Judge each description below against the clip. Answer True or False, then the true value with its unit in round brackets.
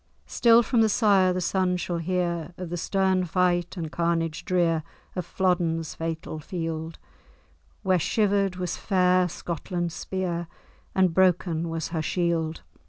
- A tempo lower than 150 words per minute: True (140 wpm)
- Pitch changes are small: True (2.1 semitones)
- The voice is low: False (175 Hz)